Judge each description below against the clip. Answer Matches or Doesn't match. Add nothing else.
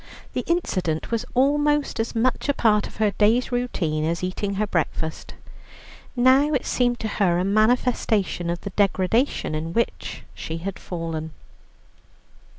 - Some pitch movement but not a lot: Doesn't match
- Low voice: Doesn't match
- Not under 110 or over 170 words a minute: Matches